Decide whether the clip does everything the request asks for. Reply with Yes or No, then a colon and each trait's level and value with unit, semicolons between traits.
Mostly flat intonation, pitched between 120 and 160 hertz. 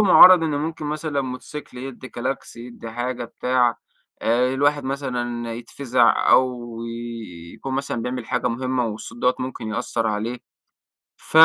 Yes: narrow, 2.2 semitones; low, 125 Hz